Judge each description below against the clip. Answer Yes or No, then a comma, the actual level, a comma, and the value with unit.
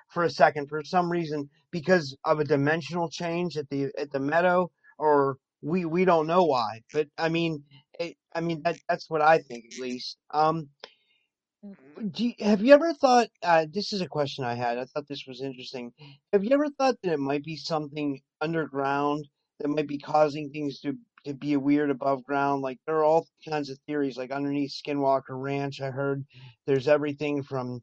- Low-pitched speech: No, medium, 150 Hz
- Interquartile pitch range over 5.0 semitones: No, average, 3.2 semitones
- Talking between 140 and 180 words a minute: No, average, 195 wpm